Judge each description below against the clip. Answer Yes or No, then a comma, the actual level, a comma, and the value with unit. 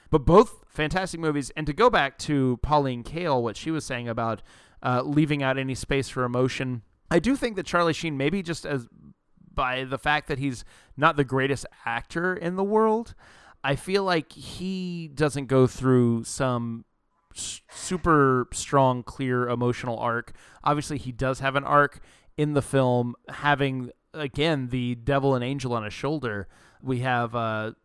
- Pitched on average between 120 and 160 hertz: Yes, low, 135 Hz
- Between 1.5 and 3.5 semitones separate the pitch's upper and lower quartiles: No, average, 3.9 semitones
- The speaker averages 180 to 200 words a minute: No, average, 170 wpm